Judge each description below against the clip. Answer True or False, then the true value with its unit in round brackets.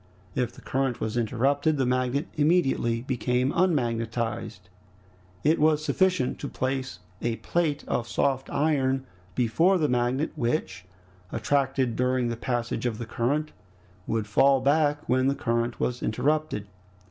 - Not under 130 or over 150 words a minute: True (135 wpm)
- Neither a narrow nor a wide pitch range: True (3.5 semitones)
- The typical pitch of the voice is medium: False (130 Hz)